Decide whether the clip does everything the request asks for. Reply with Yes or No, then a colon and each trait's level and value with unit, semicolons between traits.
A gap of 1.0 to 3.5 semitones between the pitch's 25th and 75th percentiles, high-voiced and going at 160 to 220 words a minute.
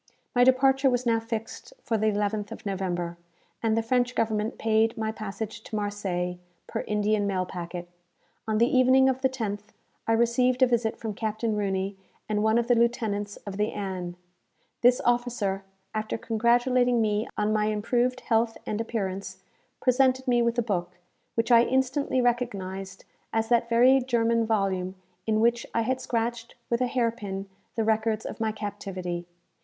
Yes: average, 2.8 semitones; high, 225 Hz; average, 170 wpm